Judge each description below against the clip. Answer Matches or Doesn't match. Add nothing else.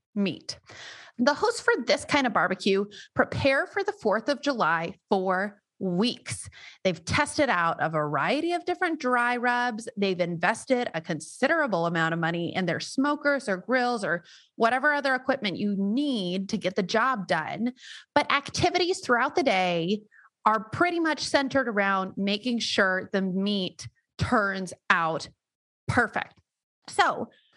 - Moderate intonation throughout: Doesn't match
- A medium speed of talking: Matches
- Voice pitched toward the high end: Matches